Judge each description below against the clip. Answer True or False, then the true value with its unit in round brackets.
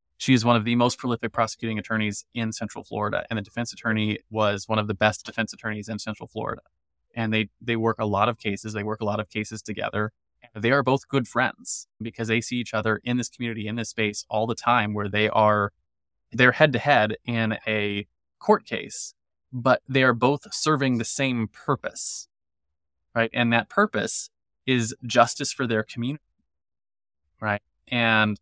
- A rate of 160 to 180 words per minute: False (190 wpm)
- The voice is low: True (110 Hz)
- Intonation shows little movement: True (2.3 semitones)